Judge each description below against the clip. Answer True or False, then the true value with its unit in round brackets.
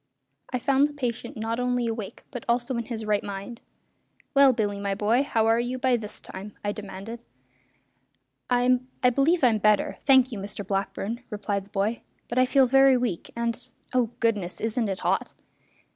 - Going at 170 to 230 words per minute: True (175 wpm)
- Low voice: False (230 Hz)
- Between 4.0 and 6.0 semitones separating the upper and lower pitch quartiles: False (3.3 semitones)